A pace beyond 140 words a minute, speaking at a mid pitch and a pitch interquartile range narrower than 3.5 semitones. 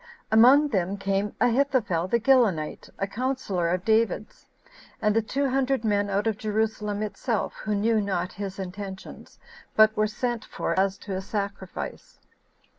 No: average, 150 wpm; high, 210 Hz; average, 2.7 semitones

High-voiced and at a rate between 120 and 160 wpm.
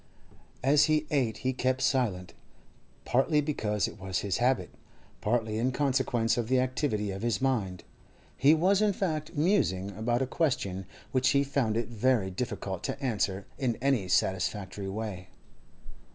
No: low, 120 Hz; average, 150 wpm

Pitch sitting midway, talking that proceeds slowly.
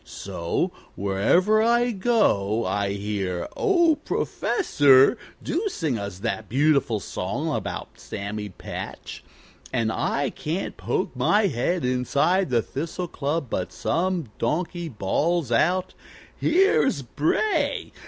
Yes: medium, 145 Hz; slow, 115 wpm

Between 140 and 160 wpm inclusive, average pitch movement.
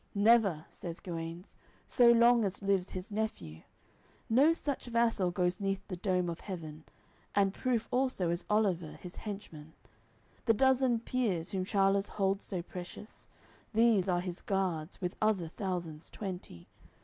Yes: average, 145 wpm; average, 3.8 semitones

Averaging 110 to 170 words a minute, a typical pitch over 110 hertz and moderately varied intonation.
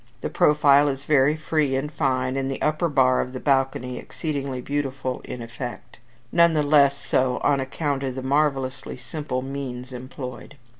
No: average, 165 wpm; low, 135 Hz; narrow, 2.2 semitones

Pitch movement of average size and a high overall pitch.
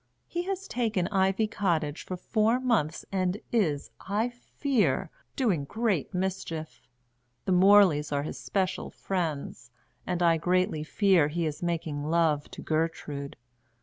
No: average, 4.8 semitones; medium, 180 Hz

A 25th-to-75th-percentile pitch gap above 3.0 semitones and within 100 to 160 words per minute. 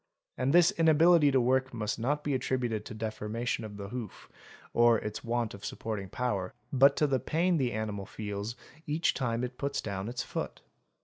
No: average, 4.3 semitones; average, 190 wpm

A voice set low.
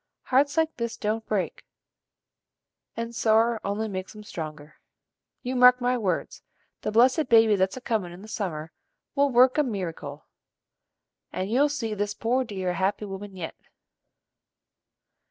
No: high, 220 Hz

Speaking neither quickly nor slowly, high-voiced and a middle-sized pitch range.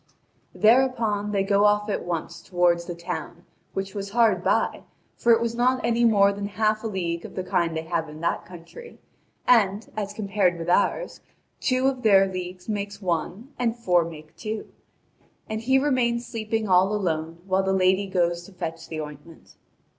Yes: average, 180 wpm; high, 200 Hz; average, 4.1 semitones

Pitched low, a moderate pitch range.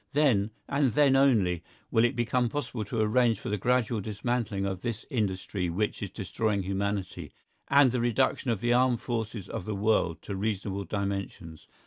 Yes: low, 110 Hz; average, 3.7 semitones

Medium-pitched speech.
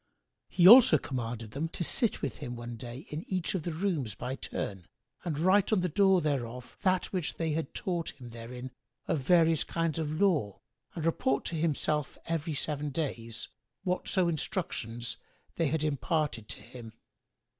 Yes: medium, 150 Hz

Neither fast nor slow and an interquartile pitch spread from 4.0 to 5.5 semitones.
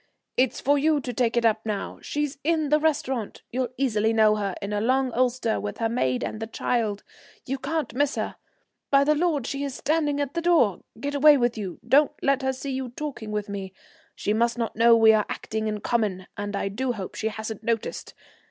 No: fast, 215 wpm; average, 4.5 semitones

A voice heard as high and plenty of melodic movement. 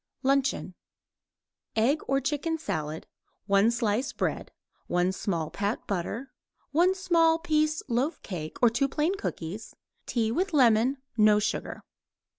Yes: high, 245 Hz; wide, 7.0 semitones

